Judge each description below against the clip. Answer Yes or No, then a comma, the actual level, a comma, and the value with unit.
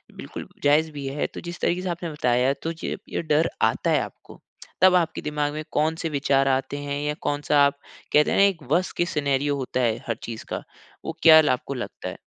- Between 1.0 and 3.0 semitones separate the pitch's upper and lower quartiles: Yes, average, 2.7 semitones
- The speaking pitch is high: No, medium, 150 Hz